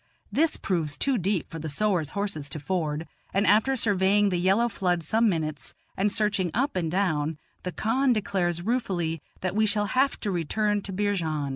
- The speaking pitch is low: No, high, 190 Hz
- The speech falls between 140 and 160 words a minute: No, average, 180 wpm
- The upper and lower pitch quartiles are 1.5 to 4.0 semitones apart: No, average, 4.4 semitones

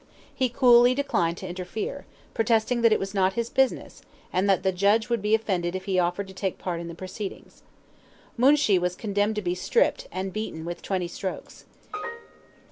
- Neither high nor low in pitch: No, high, 195 Hz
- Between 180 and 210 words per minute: Yes, average, 185 wpm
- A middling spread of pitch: Yes, average, 4.0 semitones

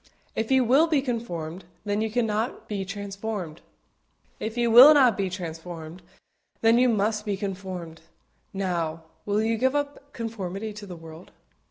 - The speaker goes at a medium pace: Yes, average, 155 wpm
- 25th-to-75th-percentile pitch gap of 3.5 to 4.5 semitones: Yes, average, 4.1 semitones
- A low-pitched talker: No, high, 210 Hz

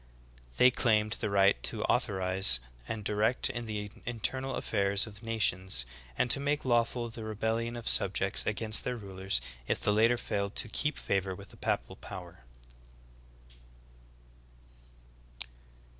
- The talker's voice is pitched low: Yes, low, 110 Hz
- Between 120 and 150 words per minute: Yes, average, 140 wpm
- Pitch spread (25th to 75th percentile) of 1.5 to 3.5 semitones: Yes, average, 3.1 semitones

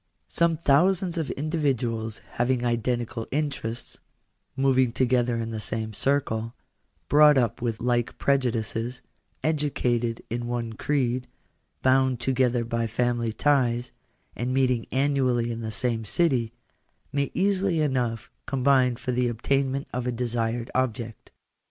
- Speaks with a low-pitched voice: Yes, low, 125 Hz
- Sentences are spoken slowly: Yes, slow, 125 wpm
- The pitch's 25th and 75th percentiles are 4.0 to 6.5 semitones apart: No, average, 2.8 semitones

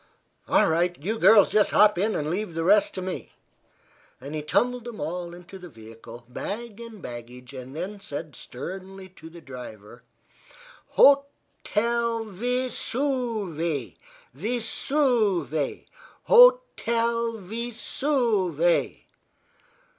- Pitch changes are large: Yes, wide, 6.6 semitones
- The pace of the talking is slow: Yes, slow, 120 wpm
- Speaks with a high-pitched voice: Yes, high, 195 Hz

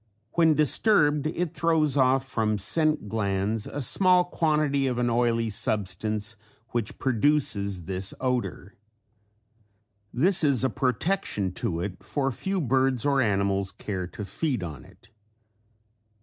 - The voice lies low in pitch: Yes, low, 125 Hz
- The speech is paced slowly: Yes, slow, 130 wpm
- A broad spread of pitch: Yes, wide, 6.6 semitones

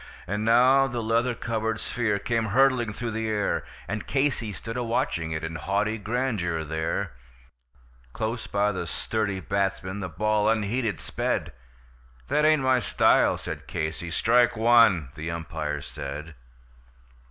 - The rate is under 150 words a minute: Yes, average, 140 wpm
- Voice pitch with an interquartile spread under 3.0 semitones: No, average, 4.8 semitones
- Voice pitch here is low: Yes, low, 110 Hz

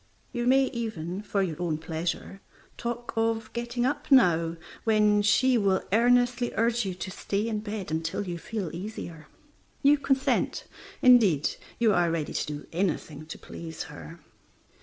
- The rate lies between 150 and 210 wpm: Yes, average, 155 wpm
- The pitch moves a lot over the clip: Yes, wide, 6.0 semitones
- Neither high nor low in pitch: No, high, 205 Hz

